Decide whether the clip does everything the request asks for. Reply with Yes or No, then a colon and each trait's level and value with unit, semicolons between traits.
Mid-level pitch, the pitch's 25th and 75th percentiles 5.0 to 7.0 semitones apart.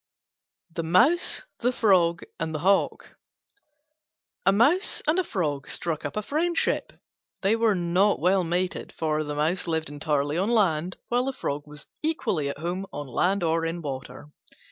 Yes: medium, 175 Hz; average, 5.3 semitones